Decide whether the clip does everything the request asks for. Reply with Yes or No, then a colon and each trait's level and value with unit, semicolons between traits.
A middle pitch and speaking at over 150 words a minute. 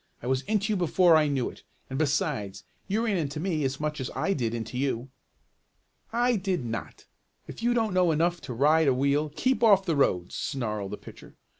Yes: medium, 150 Hz; fast, 205 wpm